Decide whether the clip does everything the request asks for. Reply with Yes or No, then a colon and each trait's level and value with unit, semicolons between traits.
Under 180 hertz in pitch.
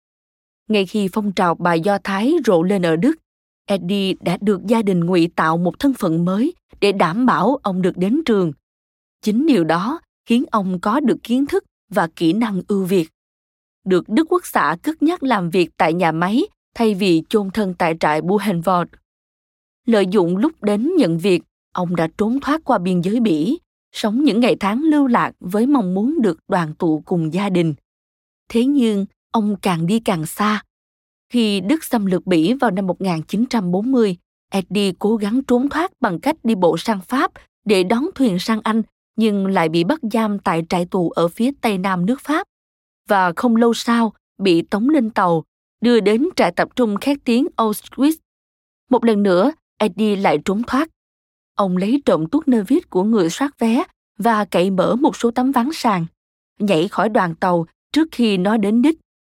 No: high, 210 Hz